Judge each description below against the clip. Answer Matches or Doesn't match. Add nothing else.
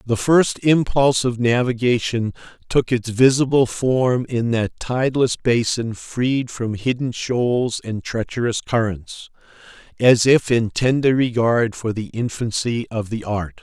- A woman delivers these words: Doesn't match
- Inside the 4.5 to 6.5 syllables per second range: Doesn't match